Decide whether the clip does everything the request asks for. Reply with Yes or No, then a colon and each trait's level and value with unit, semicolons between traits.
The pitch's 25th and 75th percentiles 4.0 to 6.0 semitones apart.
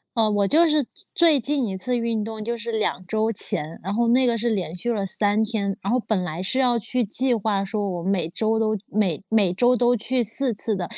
No: average, 3.3 semitones